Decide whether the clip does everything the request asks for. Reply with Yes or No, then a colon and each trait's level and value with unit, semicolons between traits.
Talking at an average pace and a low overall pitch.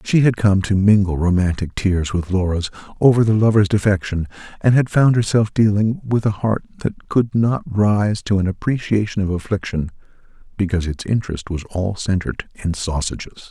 Yes: average, 170 wpm; low, 100 Hz